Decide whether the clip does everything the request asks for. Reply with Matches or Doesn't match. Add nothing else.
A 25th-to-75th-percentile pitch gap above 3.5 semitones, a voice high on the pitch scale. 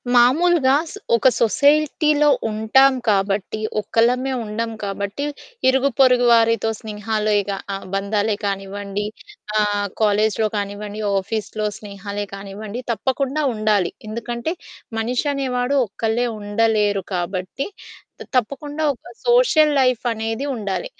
Matches